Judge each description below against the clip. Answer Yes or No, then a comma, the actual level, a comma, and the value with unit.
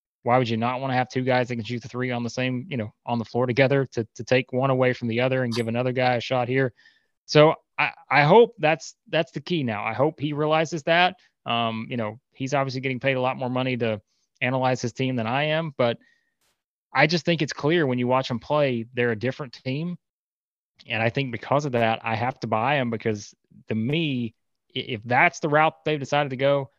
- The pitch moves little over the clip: No, average, 3.5 semitones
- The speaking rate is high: Yes, fast, 240 wpm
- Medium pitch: No, low, 130 Hz